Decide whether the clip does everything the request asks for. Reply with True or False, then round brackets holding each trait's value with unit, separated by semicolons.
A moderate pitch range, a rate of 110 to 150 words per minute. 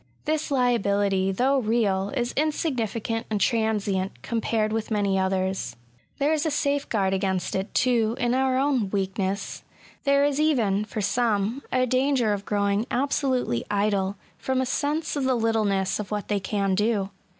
False (4.6 semitones; 160 wpm)